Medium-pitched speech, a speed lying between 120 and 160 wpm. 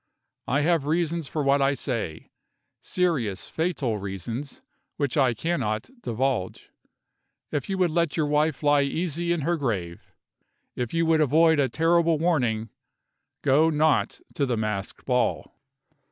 Yes: medium, 145 Hz; average, 140 wpm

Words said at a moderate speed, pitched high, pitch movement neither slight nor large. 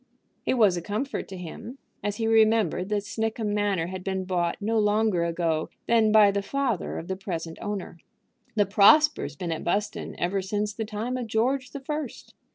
Yes: average, 185 wpm; high, 205 Hz; average, 3.2 semitones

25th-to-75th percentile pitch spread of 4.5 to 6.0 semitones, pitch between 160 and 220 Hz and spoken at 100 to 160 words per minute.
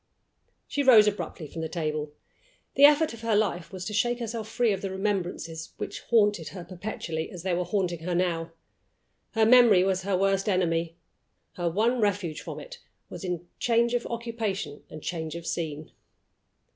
No: average, 4.8 semitones; high, 190 Hz; average, 175 wpm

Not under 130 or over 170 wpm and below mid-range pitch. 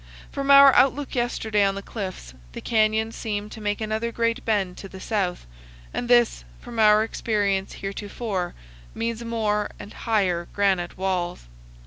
No: average, 150 wpm; high, 210 Hz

